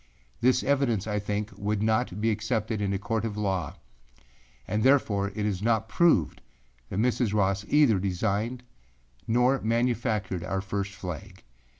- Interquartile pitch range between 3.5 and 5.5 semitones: No, average, 2.8 semitones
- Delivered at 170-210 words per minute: No, average, 150 wpm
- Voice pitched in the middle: No, low, 105 Hz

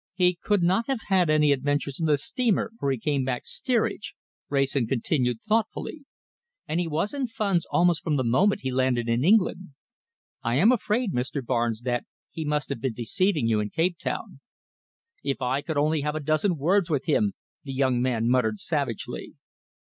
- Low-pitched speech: No, medium, 150 Hz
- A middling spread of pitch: No, wide, 6.1 semitones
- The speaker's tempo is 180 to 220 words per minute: Yes, average, 185 wpm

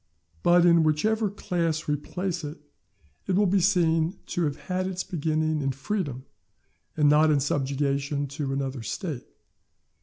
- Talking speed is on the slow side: No, average, 150 wpm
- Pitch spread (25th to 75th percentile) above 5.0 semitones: No, average, 4.1 semitones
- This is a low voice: No, medium, 155 Hz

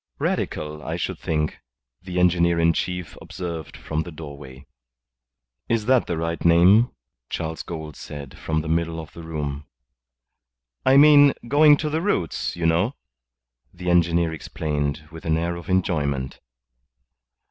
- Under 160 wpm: Yes, average, 145 wpm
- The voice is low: Yes, very low, 85 Hz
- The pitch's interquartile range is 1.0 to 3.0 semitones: Yes, narrow, 2.6 semitones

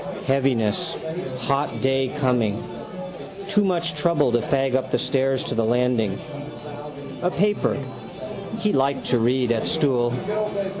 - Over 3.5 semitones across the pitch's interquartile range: No, average, 3.2 semitones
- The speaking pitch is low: Yes, low, 130 Hz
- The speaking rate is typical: No, slow, 130 wpm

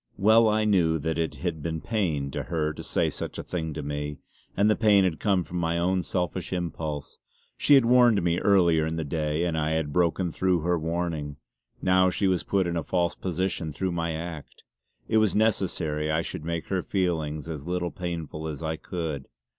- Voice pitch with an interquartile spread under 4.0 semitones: Yes, average, 2.8 semitones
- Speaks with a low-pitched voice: Yes, very low, 85 Hz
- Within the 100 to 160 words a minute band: No, fast, 205 wpm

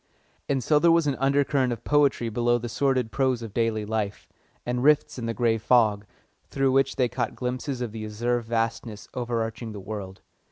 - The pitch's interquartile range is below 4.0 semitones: Yes, average, 2.9 semitones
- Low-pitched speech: Yes, low, 120 Hz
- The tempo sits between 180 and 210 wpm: Yes, average, 190 wpm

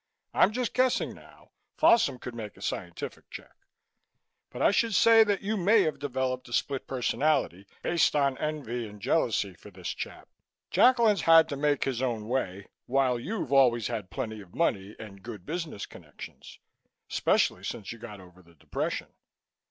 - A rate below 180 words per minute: Yes, average, 165 wpm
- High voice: No, low, 130 Hz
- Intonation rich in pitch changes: Yes, wide, 7.8 semitones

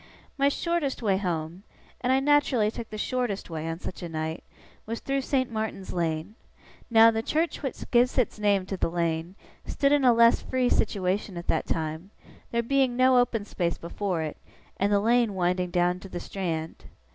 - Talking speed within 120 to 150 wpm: No, average, 190 wpm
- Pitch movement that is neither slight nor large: No, wide, 6.0 semitones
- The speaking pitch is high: Yes, high, 205 Hz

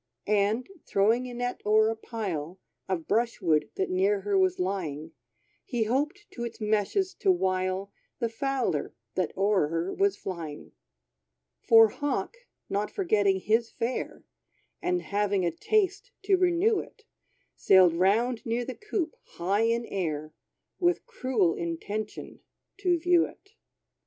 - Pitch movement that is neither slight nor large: No, wide, 6.2 semitones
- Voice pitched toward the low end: No, high, 215 Hz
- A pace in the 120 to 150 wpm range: Yes, average, 140 wpm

